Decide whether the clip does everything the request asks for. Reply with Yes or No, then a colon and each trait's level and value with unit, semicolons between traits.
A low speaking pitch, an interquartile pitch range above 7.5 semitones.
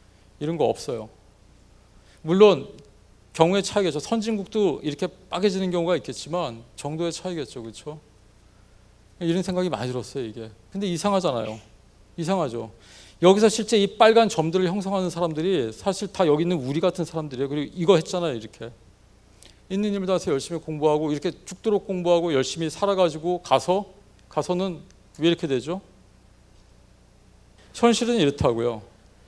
No: medium, 160 Hz; wide, 8.7 semitones